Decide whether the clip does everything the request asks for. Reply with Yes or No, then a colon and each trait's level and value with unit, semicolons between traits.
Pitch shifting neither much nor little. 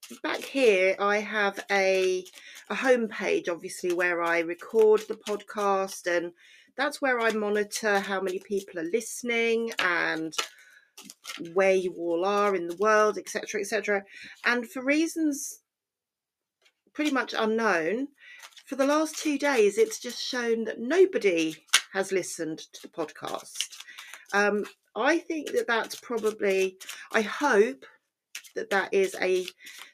No: wide, 6.3 semitones